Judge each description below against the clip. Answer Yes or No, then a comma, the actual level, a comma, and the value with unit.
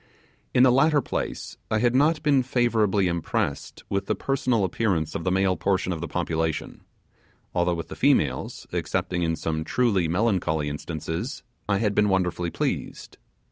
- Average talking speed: Yes, average, 160 wpm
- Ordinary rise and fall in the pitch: No, wide, 6.4 semitones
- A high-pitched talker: No, very low, 95 Hz